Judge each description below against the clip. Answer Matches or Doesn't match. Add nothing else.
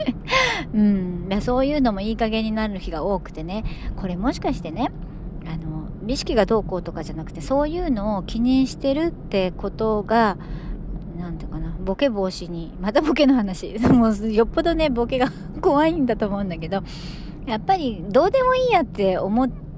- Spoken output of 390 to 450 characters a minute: Doesn't match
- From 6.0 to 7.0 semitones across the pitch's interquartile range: Matches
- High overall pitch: Matches